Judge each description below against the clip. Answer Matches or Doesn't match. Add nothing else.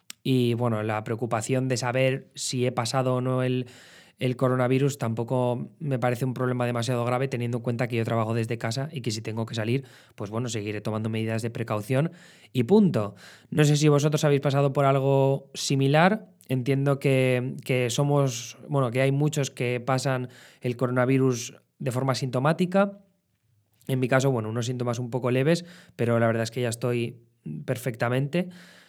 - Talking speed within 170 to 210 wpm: Matches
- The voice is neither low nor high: Doesn't match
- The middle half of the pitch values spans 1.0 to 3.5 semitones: Matches